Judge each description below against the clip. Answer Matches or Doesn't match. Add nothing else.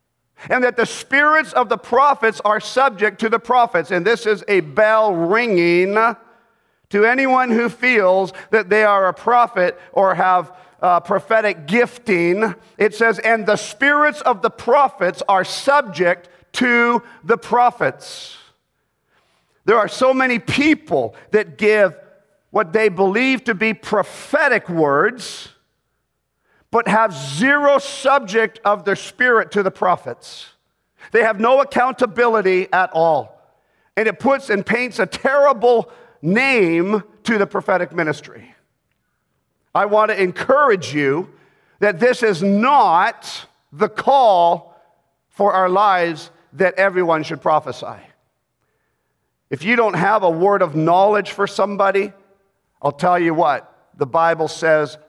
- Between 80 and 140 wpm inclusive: Matches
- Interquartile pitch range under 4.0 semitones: Doesn't match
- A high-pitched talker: Matches